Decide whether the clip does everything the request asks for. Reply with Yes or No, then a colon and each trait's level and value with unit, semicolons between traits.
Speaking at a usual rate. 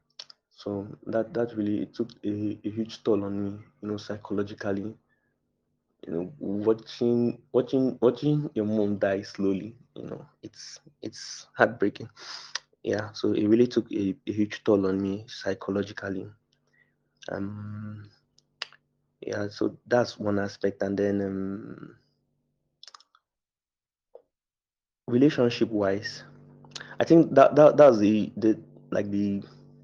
No: slow, 120 wpm